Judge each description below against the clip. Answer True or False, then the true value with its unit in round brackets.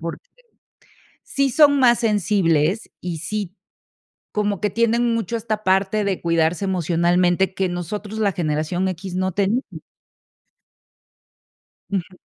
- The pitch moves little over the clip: False (3.5 semitones)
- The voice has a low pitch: False (190 Hz)